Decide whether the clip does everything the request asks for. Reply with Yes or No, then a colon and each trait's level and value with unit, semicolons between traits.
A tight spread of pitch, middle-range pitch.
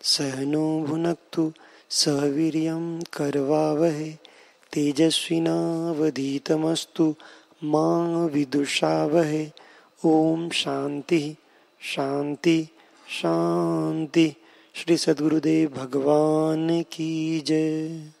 Yes: narrow, 1.9 semitones; medium, 155 Hz